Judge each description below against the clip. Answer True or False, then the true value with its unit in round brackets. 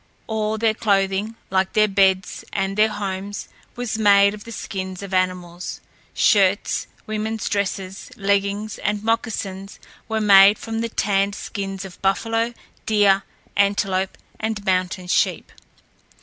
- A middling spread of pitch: False (1.9 semitones)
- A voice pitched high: True (200 Hz)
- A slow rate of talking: True (130 wpm)